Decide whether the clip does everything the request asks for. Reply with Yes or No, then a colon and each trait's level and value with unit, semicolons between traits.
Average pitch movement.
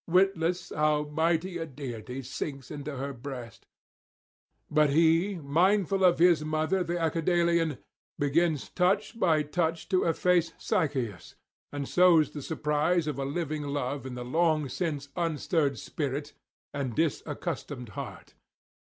Yes: average, 3.4 semitones